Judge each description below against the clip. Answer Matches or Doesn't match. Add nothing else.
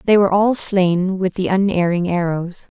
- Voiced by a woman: Matches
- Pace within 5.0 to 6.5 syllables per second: Doesn't match